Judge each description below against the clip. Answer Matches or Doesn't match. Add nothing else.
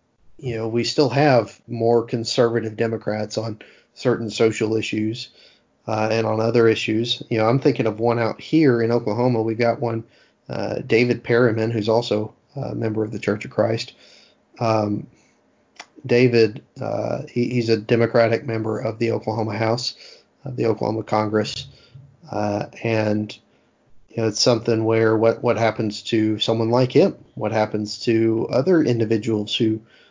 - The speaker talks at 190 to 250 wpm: Doesn't match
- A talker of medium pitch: Doesn't match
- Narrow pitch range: Matches